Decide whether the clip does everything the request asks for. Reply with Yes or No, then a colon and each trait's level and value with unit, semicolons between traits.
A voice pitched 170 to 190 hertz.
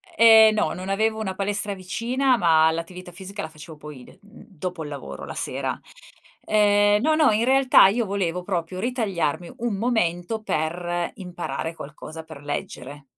Yes: medium, 185 Hz